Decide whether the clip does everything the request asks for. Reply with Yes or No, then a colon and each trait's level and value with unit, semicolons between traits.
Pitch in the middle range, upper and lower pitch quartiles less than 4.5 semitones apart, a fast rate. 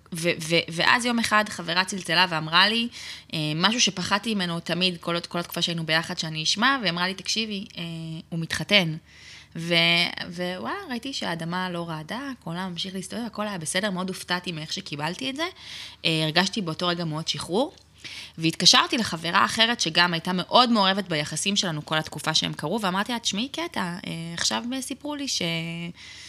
Yes: medium, 180 Hz; average, 4.1 semitones; fast, 170 wpm